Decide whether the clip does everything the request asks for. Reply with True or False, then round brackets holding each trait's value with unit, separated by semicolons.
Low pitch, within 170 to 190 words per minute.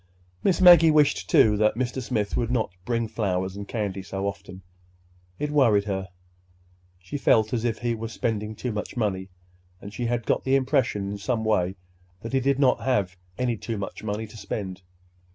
True (110 Hz; 185 wpm)